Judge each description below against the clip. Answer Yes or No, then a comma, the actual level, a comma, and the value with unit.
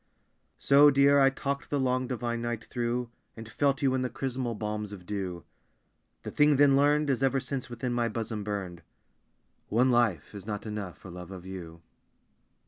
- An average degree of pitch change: Yes, average, 4.7 semitones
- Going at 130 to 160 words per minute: No, average, 180 wpm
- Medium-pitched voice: No, low, 120 Hz